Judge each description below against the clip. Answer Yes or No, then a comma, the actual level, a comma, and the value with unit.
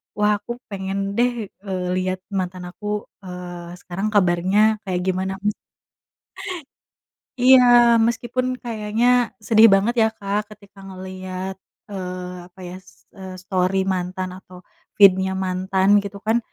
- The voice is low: No, high, 195 Hz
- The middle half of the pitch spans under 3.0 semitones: Yes, narrow, 2.6 semitones